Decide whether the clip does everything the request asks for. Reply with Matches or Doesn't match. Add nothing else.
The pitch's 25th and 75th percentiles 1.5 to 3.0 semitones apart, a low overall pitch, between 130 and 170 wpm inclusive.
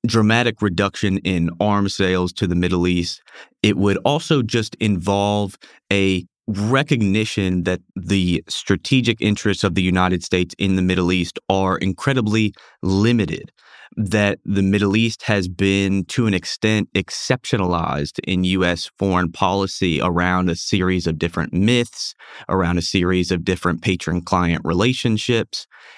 Matches